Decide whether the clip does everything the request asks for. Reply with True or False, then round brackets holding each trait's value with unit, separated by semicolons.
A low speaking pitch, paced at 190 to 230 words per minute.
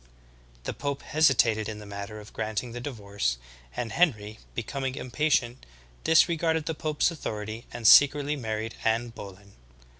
False (120 Hz; 140 wpm)